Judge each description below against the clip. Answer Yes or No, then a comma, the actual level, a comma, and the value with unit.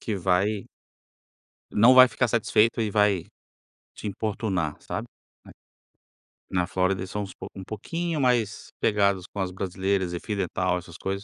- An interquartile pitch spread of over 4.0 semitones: No, average, 2.8 semitones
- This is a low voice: Yes, low, 100 Hz